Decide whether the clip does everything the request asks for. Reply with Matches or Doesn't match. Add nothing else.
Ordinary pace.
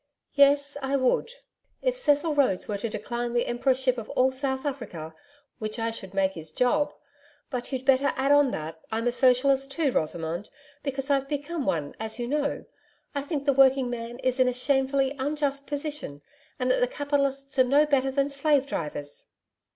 Matches